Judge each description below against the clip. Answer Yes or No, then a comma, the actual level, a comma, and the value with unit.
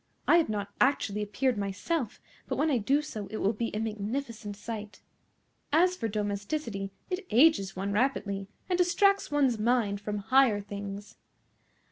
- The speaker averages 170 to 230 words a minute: No, average, 155 wpm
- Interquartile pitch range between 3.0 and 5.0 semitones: No, wide, 5.4 semitones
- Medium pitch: No, high, 215 Hz